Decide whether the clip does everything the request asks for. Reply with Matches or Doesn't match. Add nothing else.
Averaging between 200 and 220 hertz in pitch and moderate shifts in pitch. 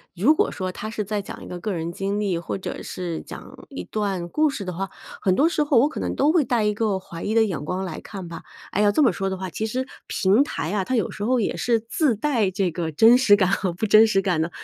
Matches